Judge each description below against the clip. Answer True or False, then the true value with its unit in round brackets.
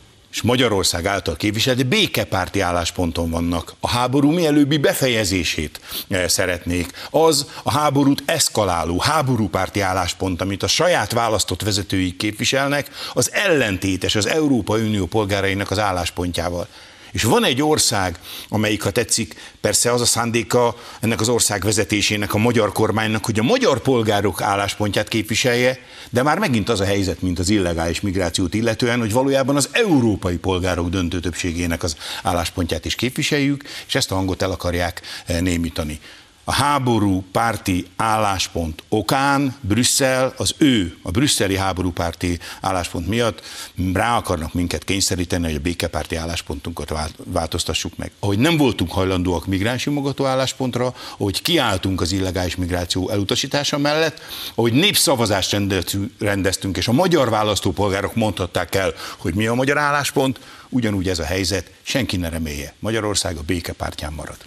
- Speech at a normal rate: True (135 wpm)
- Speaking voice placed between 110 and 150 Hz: False (100 Hz)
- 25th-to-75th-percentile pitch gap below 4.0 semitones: False (4.8 semitones)